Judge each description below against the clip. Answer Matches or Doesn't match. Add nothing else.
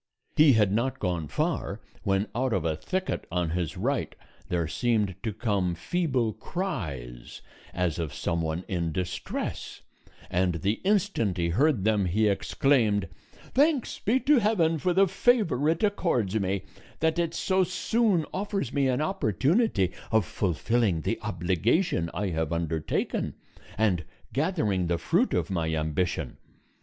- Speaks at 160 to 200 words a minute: Doesn't match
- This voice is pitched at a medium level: Doesn't match